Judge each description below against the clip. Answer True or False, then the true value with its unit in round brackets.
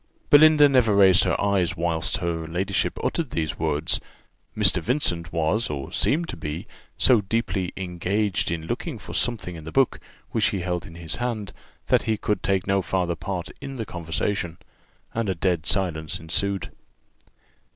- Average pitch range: True (4.1 semitones)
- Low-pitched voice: True (95 Hz)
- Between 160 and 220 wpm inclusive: True (170 wpm)